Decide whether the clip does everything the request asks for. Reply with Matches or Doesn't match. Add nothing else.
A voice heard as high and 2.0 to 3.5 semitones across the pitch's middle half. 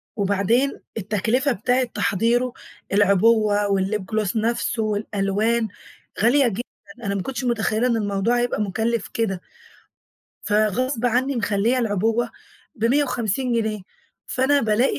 Matches